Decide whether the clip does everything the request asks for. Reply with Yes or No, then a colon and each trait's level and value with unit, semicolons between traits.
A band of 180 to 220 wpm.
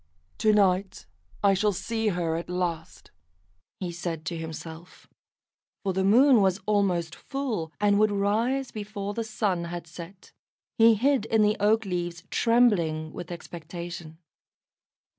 No: average, 140 wpm